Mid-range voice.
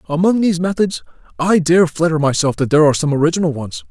Yes: medium, 160 Hz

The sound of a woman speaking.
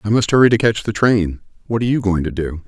No: male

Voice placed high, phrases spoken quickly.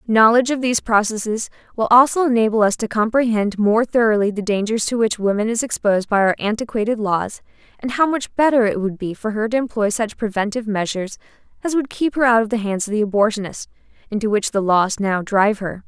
Yes: high, 220 Hz; fast, 210 wpm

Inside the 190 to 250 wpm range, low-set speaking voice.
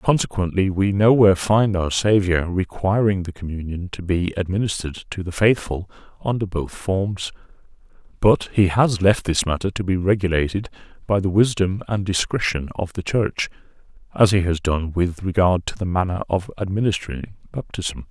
No: average, 155 wpm; very low, 95 Hz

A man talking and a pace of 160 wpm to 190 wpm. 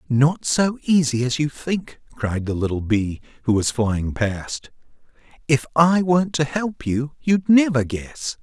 Yes: male; average, 165 wpm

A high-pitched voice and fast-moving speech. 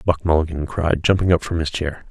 No: very low, 80 Hz; fast, 230 wpm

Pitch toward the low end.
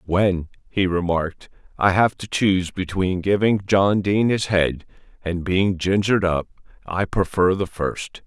Yes: very low, 95 Hz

